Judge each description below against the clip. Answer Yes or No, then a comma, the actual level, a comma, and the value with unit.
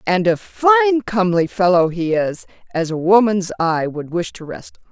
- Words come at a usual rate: Yes, average, 195 wpm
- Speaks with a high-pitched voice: Yes, high, 195 Hz